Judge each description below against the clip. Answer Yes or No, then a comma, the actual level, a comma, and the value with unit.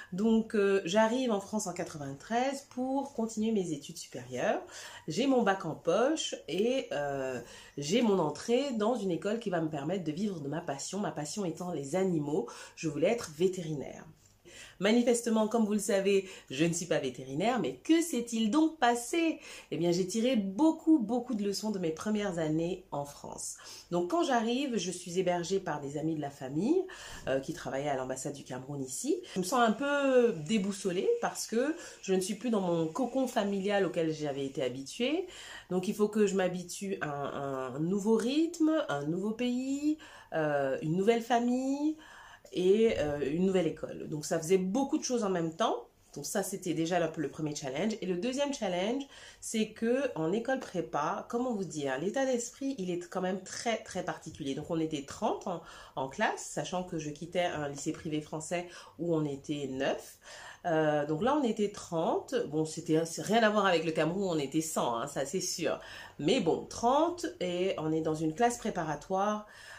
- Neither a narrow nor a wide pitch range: No, wide, 6.8 semitones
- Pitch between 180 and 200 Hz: Yes, high, 190 Hz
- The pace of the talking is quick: No, average, 195 wpm